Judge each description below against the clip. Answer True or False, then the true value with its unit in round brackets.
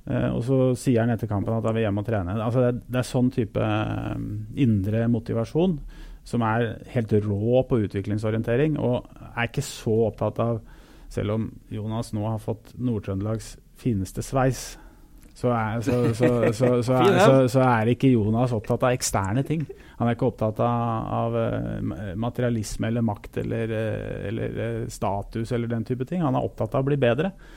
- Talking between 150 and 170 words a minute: True (155 wpm)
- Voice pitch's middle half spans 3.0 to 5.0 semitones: False (2.4 semitones)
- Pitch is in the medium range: False (115 Hz)